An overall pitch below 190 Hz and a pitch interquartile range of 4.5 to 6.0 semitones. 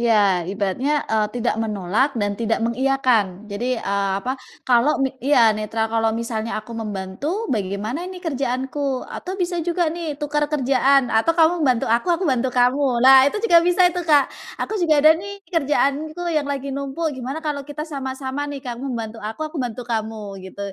No: very high, 265 Hz; average, 4.9 semitones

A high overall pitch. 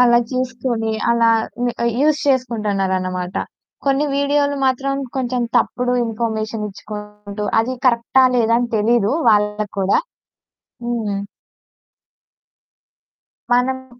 Yes: high, 235 Hz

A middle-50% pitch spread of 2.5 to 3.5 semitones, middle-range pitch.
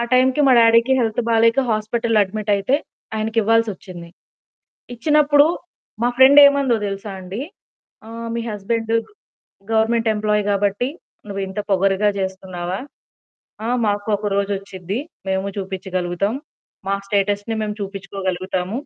No: average, 2.9 semitones; high, 210 Hz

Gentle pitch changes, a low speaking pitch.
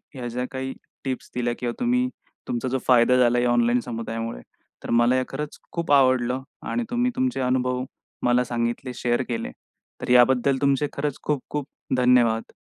Yes: narrow, 2.0 semitones; low, 125 Hz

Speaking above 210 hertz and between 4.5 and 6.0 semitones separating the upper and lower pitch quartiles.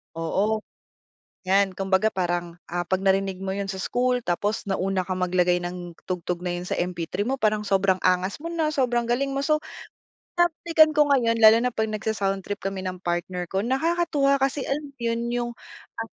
No: high, 200 Hz; average, 5.2 semitones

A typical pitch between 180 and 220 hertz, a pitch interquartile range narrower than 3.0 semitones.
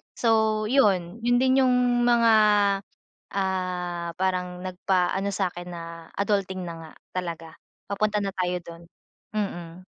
No: high, 190 Hz; average, 3.4 semitones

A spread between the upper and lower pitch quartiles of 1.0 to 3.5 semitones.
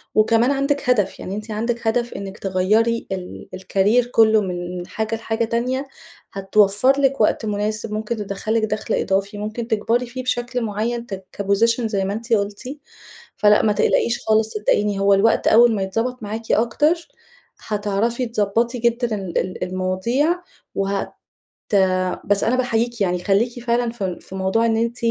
Yes: average, 3.0 semitones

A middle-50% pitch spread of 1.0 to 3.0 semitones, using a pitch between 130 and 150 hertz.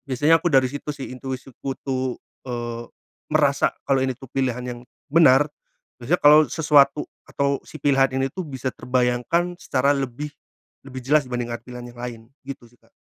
Yes: average, 2.7 semitones; low, 135 Hz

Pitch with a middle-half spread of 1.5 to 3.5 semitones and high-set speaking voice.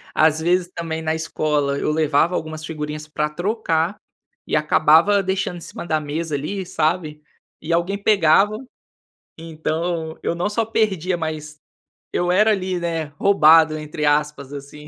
No: average, 2.8 semitones; medium, 160 Hz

